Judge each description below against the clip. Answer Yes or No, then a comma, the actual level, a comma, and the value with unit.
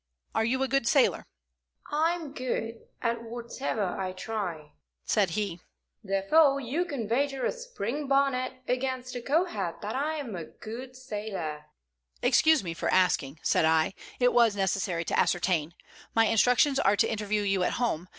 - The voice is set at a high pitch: Yes, high, 230 Hz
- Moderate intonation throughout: No, wide, 5.7 semitones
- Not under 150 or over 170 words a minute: Yes, average, 160 wpm